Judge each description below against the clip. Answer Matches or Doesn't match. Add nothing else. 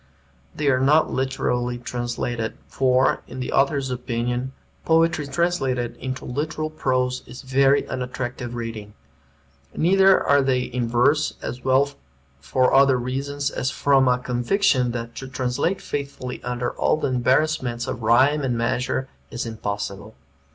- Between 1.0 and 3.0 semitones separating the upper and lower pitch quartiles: Matches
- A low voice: Matches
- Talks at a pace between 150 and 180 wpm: Doesn't match